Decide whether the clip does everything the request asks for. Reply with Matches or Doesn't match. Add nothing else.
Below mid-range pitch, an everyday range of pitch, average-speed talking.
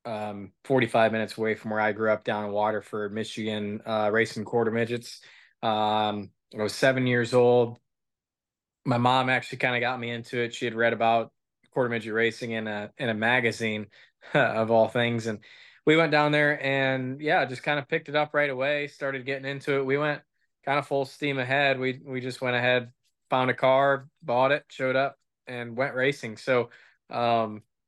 Matches